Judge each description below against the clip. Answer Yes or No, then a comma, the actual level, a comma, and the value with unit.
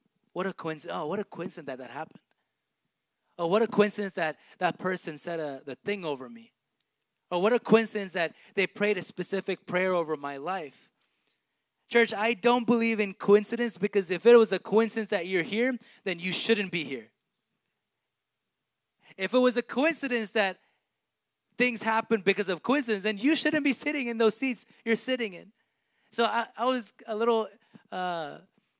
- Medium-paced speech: Yes, average, 175 wpm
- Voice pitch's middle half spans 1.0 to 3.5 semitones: No, average, 4.2 semitones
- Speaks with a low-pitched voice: No, high, 210 Hz